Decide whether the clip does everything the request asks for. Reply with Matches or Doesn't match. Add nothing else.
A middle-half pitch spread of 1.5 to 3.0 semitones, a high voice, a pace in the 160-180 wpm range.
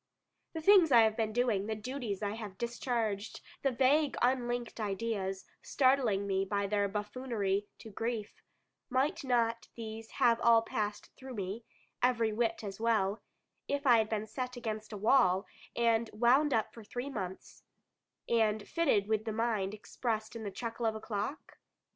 Matches